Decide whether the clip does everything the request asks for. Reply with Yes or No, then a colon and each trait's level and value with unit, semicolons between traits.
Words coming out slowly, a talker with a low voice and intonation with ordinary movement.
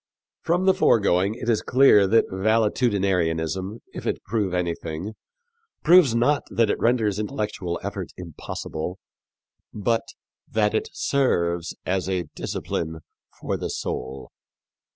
Yes: slow, 120 wpm; low, 100 Hz; average, 4.6 semitones